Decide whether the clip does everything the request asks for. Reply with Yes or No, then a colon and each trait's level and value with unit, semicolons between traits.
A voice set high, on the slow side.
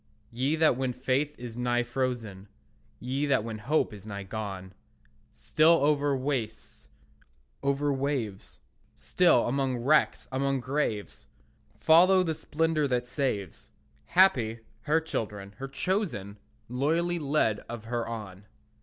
No: low, 130 Hz; slow, 125 wpm